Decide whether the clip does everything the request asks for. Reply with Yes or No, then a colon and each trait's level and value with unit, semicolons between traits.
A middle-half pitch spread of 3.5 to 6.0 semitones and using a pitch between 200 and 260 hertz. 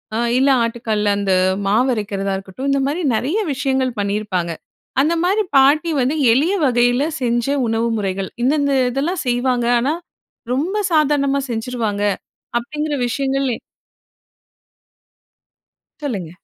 Yes: average, 4.5 semitones; very high, 250 Hz